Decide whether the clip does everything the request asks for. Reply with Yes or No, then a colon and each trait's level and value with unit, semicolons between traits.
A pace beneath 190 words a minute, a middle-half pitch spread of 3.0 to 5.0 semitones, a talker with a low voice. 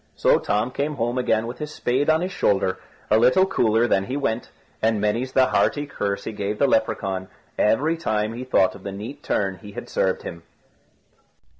No: average, 195 wpm; average, 4.3 semitones; low, 115 Hz